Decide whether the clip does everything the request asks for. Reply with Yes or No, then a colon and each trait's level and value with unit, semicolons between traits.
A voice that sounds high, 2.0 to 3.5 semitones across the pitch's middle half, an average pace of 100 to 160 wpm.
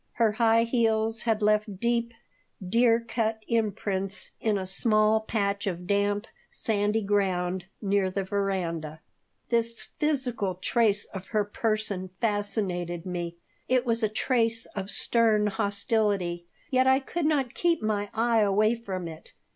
Yes: high, 215 Hz; average, 2.8 semitones; average, 140 wpm